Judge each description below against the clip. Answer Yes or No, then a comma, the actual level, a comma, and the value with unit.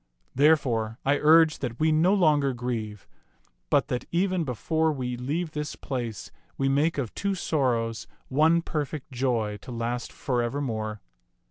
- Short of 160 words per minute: Yes, average, 145 wpm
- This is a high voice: No, low, 135 Hz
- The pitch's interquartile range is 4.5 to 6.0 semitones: Yes, average, 4.8 semitones